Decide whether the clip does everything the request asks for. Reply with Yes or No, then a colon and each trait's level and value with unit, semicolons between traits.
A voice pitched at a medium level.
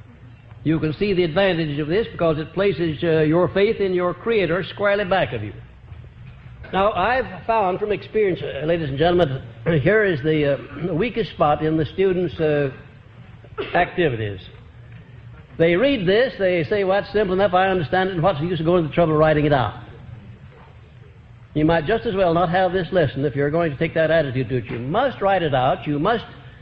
Yes: medium, 165 Hz